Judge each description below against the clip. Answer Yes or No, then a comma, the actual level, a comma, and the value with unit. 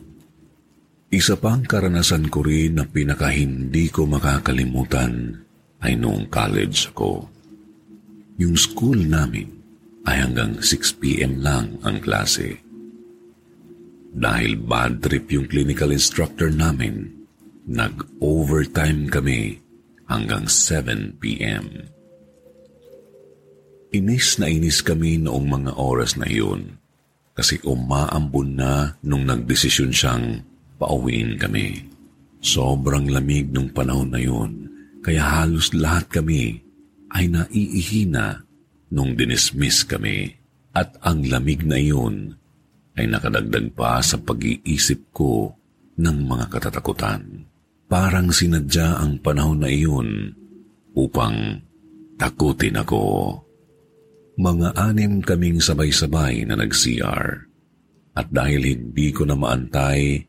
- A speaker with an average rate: No, slow, 100 wpm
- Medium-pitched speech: No, very low, 80 Hz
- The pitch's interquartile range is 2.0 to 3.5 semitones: No, average, 5.2 semitones